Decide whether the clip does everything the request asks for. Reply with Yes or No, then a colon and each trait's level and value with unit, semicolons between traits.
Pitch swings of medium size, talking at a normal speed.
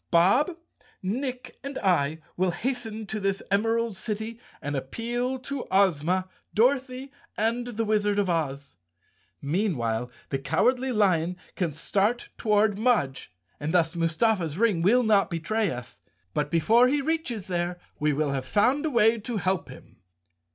No: wide, 6.1 semitones; average, 145 wpm